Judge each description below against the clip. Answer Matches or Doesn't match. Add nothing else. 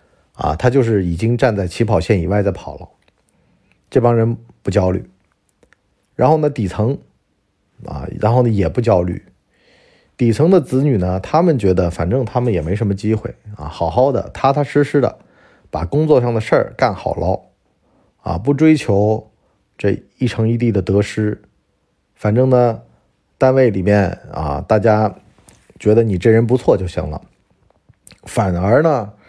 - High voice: Doesn't match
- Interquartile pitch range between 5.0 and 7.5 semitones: Doesn't match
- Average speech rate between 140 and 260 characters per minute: Matches